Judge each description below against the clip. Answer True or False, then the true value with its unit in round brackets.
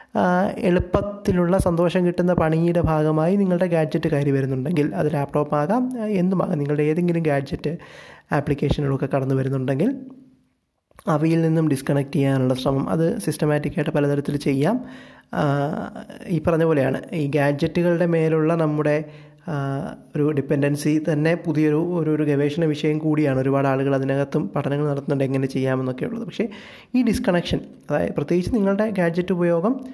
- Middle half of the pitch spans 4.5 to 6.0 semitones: False (3.7 semitones)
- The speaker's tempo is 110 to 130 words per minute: True (120 wpm)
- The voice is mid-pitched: True (155 Hz)